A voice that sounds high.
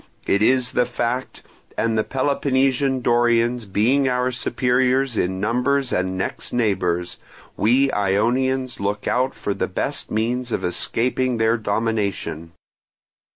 No: low, 120 Hz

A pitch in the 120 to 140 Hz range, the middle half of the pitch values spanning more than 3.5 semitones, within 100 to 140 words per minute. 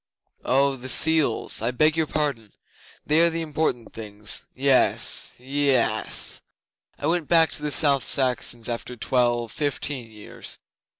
Yes: low, 135 Hz; average, 4.0 semitones; slow, 135 wpm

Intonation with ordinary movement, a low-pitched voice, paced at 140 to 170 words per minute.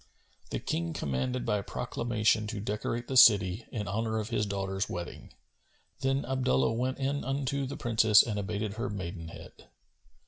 Yes: average, 3.9 semitones; low, 110 Hz; average, 150 wpm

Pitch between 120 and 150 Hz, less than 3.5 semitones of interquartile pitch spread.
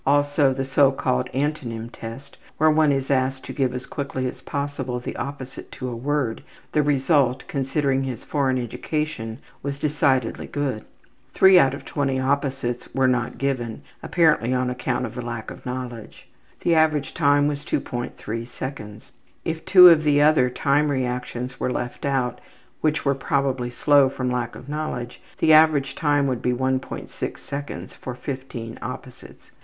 Yes: low, 135 Hz; narrow, 2.5 semitones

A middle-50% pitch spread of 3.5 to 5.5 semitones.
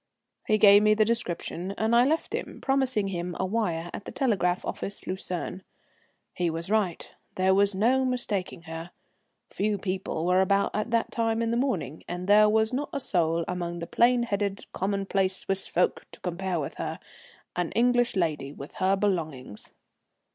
Yes: average, 3.8 semitones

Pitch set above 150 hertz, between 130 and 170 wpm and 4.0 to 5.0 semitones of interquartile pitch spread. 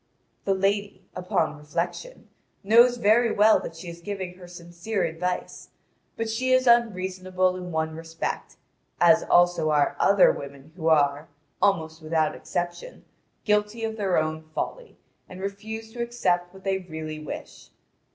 Yes: medium, 185 Hz; average, 145 wpm; average, 4.3 semitones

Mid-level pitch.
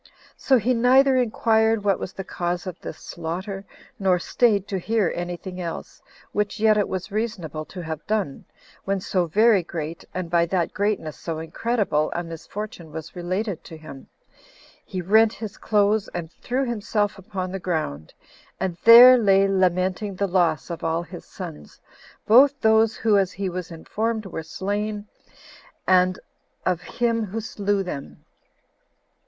No: high, 195 Hz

